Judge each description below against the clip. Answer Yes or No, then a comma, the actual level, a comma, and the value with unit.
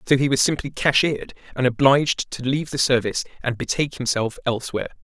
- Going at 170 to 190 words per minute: Yes, average, 175 wpm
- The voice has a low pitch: Yes, low, 130 Hz